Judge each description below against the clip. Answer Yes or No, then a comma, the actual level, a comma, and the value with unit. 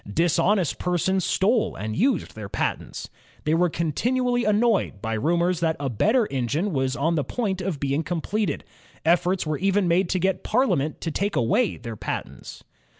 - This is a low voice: No, medium, 175 Hz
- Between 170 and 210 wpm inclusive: Yes, average, 180 wpm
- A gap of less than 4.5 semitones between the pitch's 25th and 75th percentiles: No, wide, 5.6 semitones